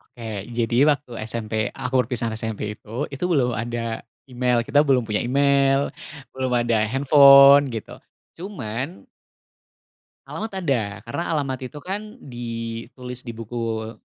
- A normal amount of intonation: Yes, average, 3.3 semitones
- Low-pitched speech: Yes, low, 125 Hz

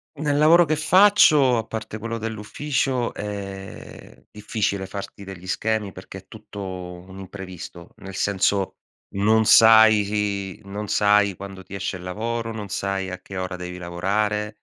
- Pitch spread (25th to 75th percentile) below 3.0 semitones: Yes, narrow, 2.6 semitones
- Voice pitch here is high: No, low, 100 Hz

